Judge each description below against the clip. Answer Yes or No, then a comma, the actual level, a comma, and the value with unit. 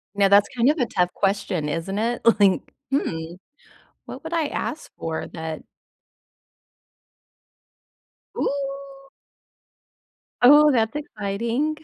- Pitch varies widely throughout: Yes, wide, 6.3 semitones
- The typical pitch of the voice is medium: No, high, 225 Hz